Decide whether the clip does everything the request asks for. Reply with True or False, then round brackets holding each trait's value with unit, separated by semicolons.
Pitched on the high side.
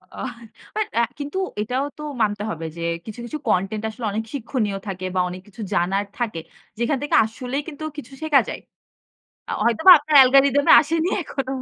True (245 Hz)